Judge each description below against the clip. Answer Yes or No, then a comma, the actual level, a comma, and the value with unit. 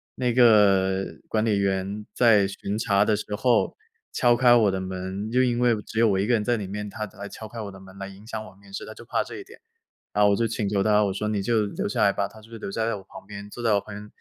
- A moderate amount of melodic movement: No, narrow, 2.3 semitones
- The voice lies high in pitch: No, low, 105 Hz